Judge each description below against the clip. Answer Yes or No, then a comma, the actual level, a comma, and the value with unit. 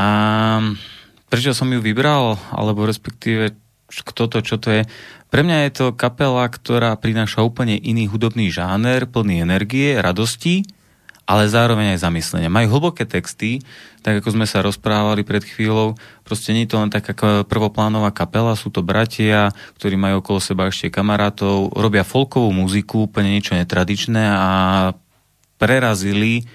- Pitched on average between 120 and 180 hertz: No, low, 110 Hz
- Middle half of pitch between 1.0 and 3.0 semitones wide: Yes, narrow, 2.4 semitones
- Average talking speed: Yes, average, 145 wpm